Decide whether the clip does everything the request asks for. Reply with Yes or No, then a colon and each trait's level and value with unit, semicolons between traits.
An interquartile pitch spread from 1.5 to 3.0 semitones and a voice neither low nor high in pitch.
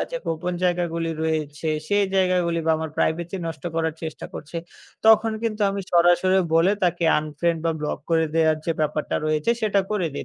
Yes: narrow, 2.4 semitones; medium, 170 Hz